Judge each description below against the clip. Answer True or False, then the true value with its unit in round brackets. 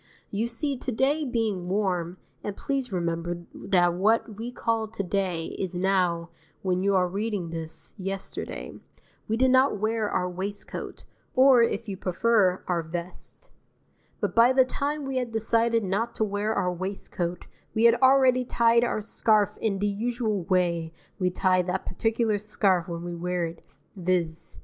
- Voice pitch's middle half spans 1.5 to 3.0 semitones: False (4.3 semitones)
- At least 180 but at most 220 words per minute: False (165 wpm)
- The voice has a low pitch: False (200 Hz)